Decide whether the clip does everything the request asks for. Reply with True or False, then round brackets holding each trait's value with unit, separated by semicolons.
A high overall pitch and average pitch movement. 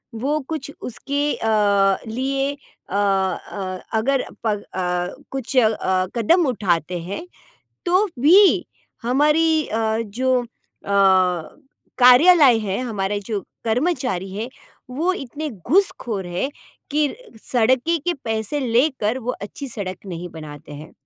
False (235 Hz; 6.1 semitones)